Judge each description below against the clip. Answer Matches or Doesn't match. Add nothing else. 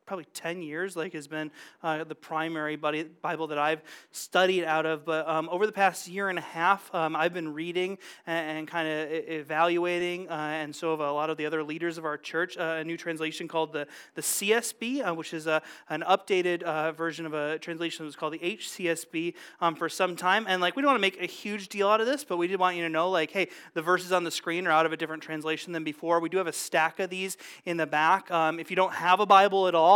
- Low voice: Doesn't match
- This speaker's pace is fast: Matches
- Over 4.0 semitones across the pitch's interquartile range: Doesn't match